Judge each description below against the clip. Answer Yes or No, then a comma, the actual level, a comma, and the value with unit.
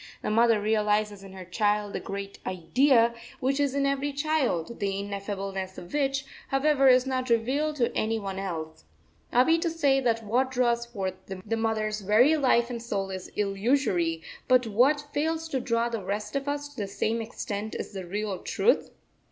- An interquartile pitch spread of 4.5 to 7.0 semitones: Yes, average, 5.2 semitones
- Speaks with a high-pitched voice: Yes, high, 230 Hz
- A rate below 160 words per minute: No, average, 185 wpm